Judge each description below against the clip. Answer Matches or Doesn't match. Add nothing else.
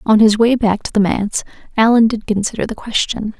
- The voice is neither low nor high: Doesn't match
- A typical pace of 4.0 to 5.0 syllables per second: Doesn't match